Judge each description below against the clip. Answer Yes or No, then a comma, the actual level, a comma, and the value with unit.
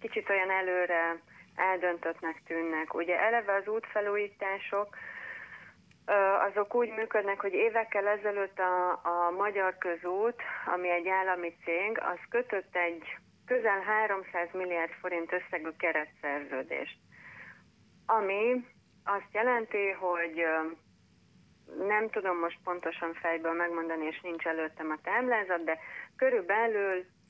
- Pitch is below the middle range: No, medium, 185 Hz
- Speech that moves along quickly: No, average, 110 wpm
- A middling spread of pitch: Yes, average, 3.6 semitones